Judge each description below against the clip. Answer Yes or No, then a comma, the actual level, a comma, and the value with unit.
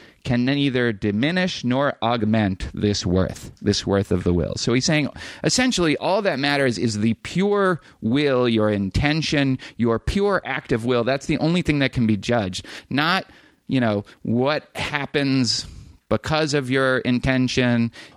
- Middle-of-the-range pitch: No, low, 125 Hz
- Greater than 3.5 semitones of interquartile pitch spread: Yes, average, 4.8 semitones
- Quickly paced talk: No, average, 155 wpm